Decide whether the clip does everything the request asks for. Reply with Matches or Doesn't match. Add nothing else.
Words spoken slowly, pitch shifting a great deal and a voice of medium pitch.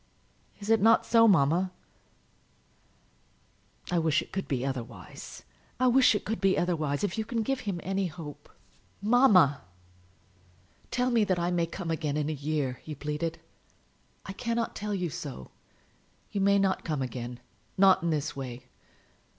Doesn't match